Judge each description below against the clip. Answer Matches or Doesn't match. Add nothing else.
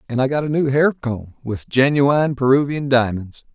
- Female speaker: Doesn't match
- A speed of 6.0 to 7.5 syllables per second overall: Doesn't match